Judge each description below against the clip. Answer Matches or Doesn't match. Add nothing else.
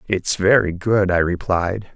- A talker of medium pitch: Doesn't match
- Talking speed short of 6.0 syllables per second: Matches